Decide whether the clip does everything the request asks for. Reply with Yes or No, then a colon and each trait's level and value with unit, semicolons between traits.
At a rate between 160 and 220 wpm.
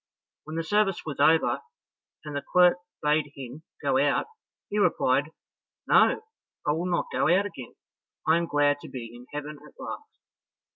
Yes: average, 165 wpm